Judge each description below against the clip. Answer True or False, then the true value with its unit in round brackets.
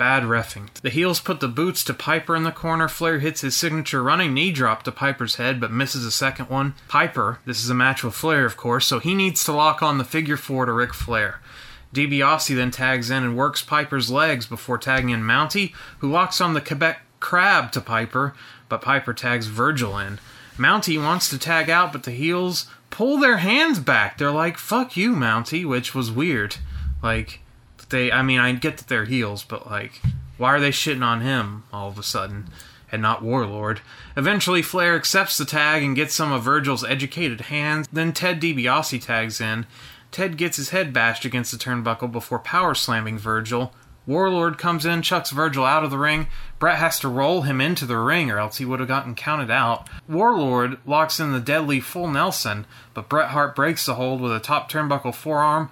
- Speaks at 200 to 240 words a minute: True (205 wpm)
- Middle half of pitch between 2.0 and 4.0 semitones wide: False (4.6 semitones)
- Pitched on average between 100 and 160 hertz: True (135 Hz)